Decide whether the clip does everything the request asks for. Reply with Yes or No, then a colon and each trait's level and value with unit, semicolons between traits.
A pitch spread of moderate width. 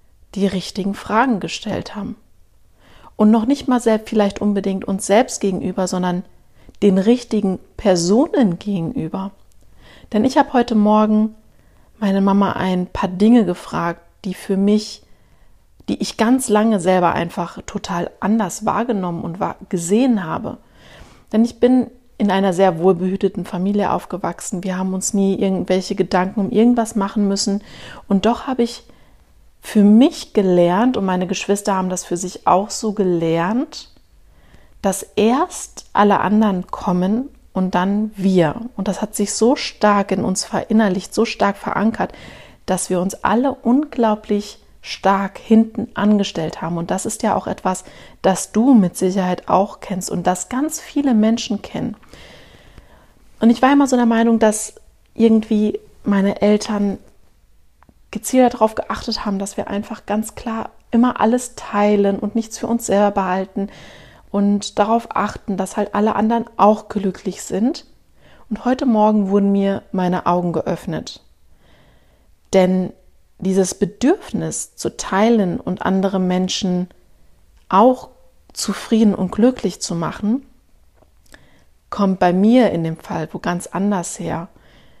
Yes: average, 3.0 semitones